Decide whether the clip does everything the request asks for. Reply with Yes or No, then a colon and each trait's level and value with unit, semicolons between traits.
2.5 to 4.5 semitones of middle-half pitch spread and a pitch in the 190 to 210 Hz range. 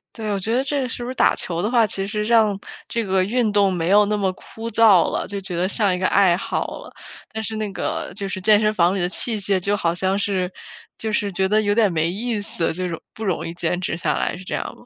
Yes: average, 2.8 semitones; high, 200 Hz